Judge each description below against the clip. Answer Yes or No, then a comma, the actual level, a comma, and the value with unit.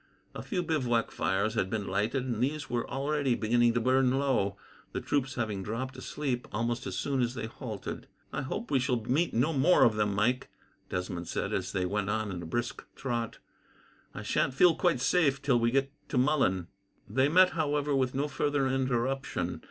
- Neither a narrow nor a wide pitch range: Yes, average, 3.9 semitones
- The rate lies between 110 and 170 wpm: No, average, 190 wpm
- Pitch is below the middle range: Yes, low, 125 Hz